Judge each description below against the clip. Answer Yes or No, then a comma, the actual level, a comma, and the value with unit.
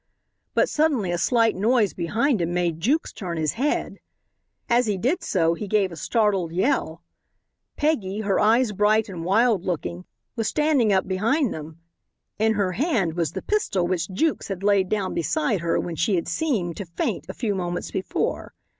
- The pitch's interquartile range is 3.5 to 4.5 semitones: No, average, 4.9 semitones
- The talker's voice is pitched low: No, high, 200 Hz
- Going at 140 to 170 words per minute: No, average, 180 wpm